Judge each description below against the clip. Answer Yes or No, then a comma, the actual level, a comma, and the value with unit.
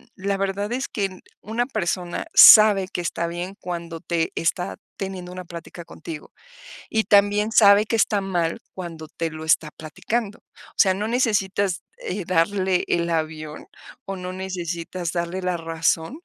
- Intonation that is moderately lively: Yes, average, 3.1 semitones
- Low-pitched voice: No, medium, 185 Hz